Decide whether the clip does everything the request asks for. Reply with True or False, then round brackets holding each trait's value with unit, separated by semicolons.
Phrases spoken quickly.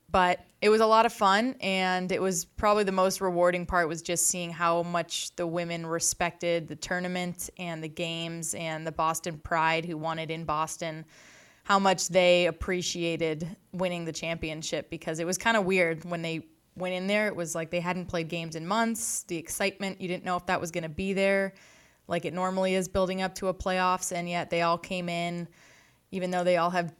True (210 wpm)